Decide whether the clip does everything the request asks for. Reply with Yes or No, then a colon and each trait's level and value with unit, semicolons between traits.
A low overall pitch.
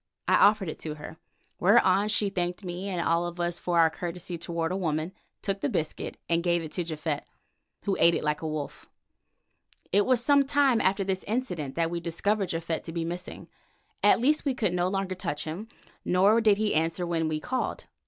No: medium, 175 Hz